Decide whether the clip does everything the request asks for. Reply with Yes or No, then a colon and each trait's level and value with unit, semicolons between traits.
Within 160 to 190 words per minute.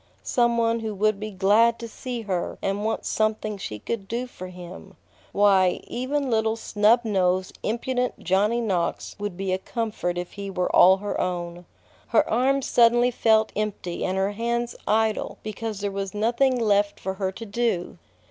Yes: average, 175 wpm